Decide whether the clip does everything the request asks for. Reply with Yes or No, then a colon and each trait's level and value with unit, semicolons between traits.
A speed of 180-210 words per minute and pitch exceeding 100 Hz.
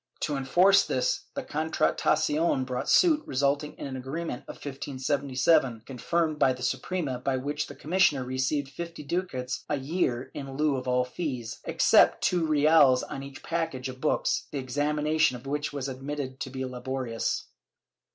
No: average, 160 wpm; medium, 140 Hz